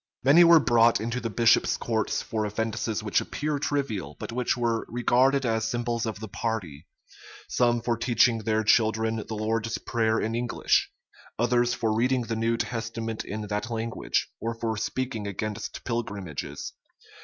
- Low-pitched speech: Yes, low, 115 Hz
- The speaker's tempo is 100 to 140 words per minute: No, average, 155 wpm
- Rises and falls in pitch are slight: Yes, narrow, 1.5 semitones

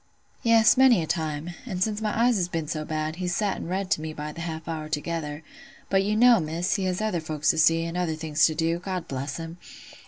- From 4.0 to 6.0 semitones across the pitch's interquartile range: No, average, 3.5 semitones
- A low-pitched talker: No, medium, 165 Hz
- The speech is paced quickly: Yes, fast, 240 wpm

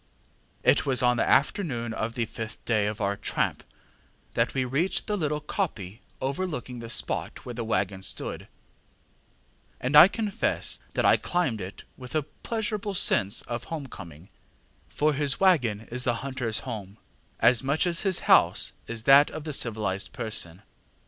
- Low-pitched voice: Yes, low, 125 Hz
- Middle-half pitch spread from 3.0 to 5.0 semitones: No, wide, 5.6 semitones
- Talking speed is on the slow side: No, average, 160 wpm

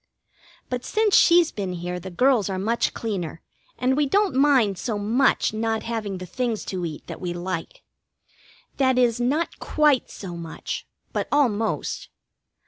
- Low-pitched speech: No, high, 225 Hz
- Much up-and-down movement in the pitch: Yes, wide, 5.9 semitones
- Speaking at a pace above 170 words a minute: No, average, 155 wpm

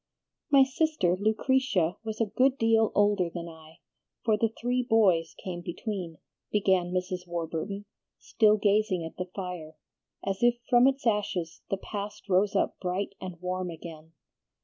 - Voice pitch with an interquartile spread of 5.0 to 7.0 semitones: No, average, 4.0 semitones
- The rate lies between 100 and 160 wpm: Yes, average, 150 wpm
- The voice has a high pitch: Yes, high, 195 Hz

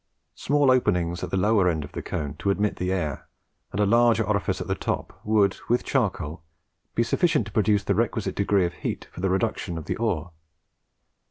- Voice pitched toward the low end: Yes, low, 100 Hz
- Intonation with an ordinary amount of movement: Yes, average, 4.0 semitones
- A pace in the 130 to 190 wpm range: No, average, 200 wpm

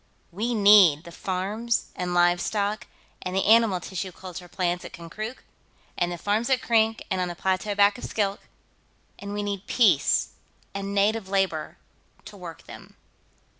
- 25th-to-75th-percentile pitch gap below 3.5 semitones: Yes, average, 2.9 semitones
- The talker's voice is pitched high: Yes, high, 200 Hz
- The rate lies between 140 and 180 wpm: Yes, average, 160 wpm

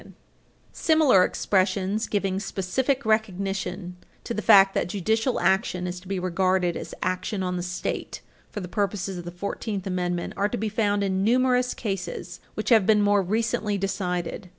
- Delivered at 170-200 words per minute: Yes, average, 175 wpm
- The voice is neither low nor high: No, high, 195 Hz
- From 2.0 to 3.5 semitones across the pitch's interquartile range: Yes, average, 2.8 semitones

